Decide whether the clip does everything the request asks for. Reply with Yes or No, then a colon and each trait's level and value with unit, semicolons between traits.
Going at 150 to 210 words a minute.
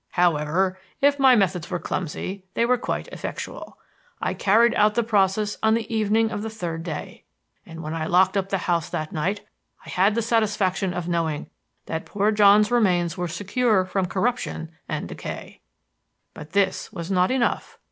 Yes: average, 175 wpm